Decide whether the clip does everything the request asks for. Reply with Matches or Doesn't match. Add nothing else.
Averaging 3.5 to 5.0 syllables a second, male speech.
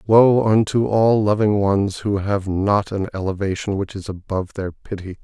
Matches